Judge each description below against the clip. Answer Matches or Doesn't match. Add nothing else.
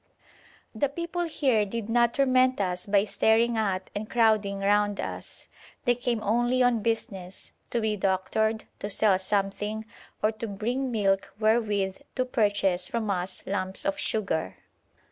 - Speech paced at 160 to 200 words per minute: Doesn't match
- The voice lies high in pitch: Matches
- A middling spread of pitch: Matches